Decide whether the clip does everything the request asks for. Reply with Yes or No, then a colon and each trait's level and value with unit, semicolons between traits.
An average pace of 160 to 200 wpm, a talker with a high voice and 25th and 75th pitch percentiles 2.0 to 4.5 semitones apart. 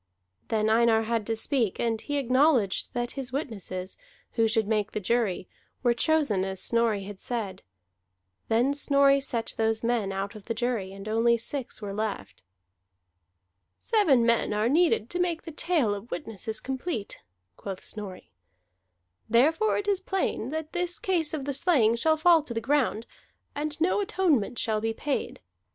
No: average, 165 wpm; high, 235 Hz; average, 5.3 semitones